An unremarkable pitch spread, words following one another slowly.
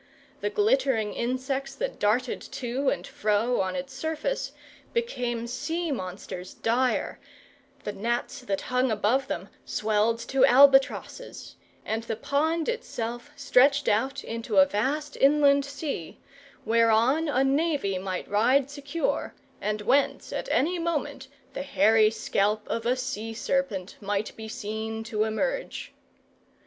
Yes: average, 4.4 semitones; slow, 130 wpm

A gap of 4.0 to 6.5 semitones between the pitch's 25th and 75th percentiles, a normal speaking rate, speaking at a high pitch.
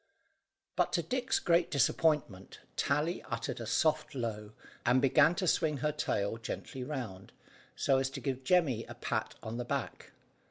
No: average, 5.1 semitones; average, 160 wpm; low, 135 Hz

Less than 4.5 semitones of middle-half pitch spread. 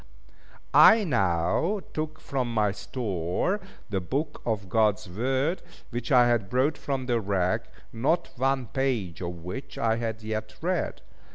No: average, 5.3 semitones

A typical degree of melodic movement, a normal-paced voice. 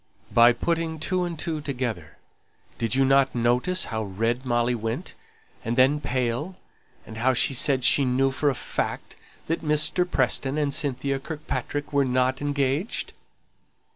Yes: average, 3.5 semitones; average, 145 wpm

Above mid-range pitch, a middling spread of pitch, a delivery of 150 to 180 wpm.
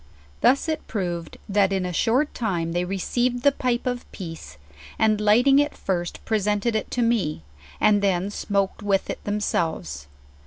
Yes: high, 205 Hz; average, 5.0 semitones; average, 160 wpm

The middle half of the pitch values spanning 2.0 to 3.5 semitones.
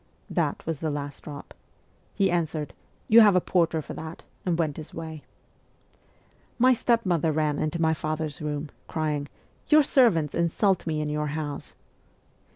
Yes: narrow, 2.6 semitones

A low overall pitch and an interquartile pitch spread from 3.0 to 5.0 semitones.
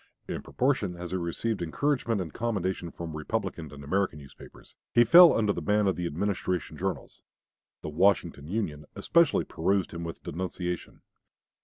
Yes: very low, 90 Hz; average, 4.2 semitones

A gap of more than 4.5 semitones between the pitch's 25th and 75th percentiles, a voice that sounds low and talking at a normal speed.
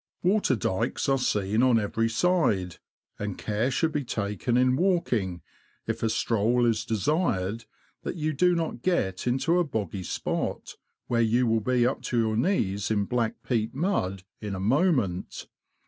Yes: average, 4.9 semitones; low, 115 Hz; average, 165 wpm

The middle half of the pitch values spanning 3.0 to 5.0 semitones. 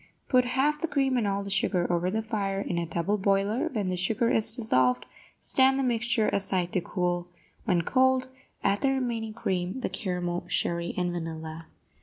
No: wide, 5.4 semitones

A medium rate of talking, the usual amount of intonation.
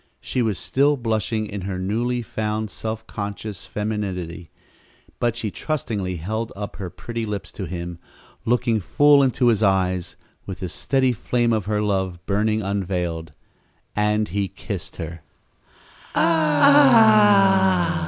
No: slow, 130 wpm; average, 3.3 semitones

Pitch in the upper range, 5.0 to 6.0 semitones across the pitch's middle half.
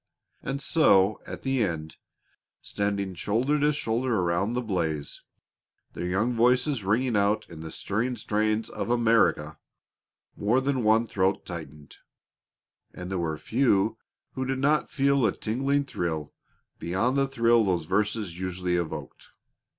No: low, 110 Hz; wide, 5.4 semitones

